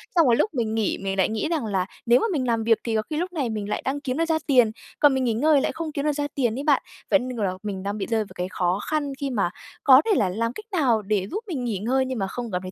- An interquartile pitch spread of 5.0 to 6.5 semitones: Yes, average, 5.3 semitones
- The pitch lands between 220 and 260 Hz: Yes, high, 240 Hz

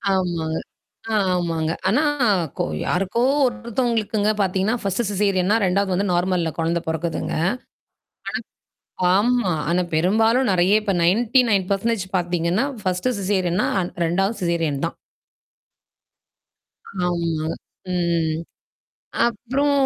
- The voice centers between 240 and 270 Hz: No, medium, 185 Hz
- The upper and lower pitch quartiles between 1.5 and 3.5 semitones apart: No, average, 3.9 semitones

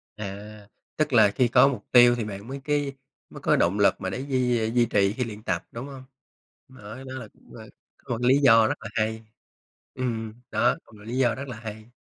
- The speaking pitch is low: Yes, low, 115 Hz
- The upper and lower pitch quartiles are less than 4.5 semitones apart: Yes, average, 3.3 semitones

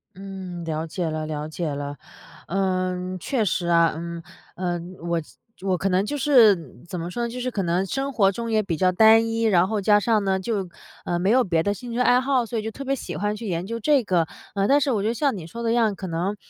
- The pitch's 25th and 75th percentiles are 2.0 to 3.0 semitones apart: No, average, 4.8 semitones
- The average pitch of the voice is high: Yes, high, 195 Hz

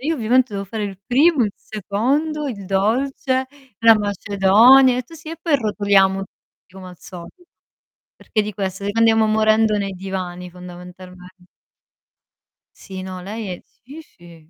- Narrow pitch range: No, average, 4.7 semitones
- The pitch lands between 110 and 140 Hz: No, high, 205 Hz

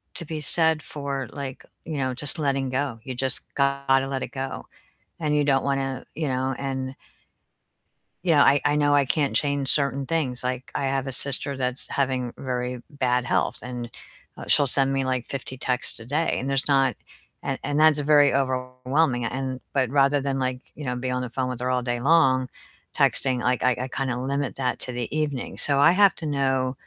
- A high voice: No, low, 135 Hz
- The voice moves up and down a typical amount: No, narrow, 1.8 semitones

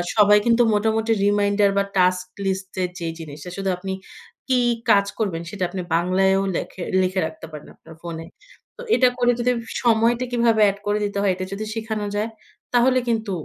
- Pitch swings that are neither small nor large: Yes, average, 3.2 semitones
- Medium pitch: No, high, 200 Hz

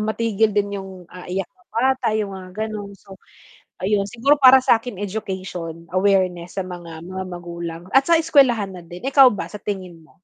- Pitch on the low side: No, high, 195 Hz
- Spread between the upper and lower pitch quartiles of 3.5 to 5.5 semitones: Yes, average, 3.8 semitones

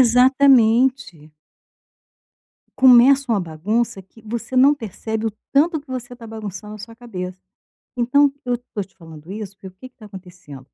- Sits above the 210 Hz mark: Yes, high, 225 Hz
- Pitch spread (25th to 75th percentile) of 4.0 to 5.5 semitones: Yes, average, 4.9 semitones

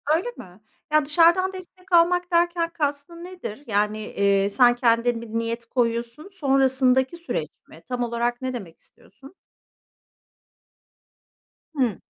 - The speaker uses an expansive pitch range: Yes, wide, 6.6 semitones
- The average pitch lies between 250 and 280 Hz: Yes, very high, 255 Hz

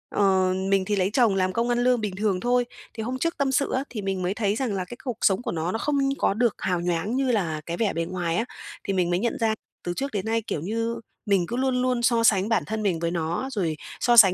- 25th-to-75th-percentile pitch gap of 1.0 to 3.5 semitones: No, average, 4.6 semitones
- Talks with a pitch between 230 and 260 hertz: No, high, 210 Hz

